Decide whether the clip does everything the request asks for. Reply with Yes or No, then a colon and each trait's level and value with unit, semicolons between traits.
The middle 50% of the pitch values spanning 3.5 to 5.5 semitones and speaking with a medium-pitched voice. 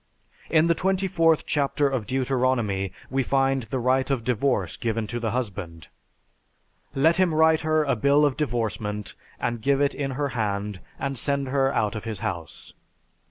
No: average, 4.5 semitones; low, 130 Hz